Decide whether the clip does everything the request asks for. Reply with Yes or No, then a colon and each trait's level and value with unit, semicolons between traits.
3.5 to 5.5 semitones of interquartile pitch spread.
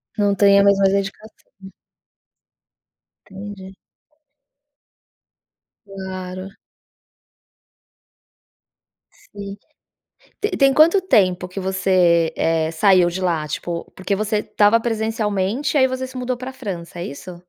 No: average, 3.0 semitones